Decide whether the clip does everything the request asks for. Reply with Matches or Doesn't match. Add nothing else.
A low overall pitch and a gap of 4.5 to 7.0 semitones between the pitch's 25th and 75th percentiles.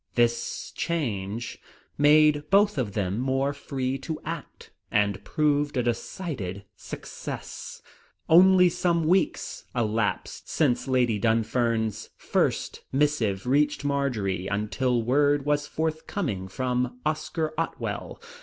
Matches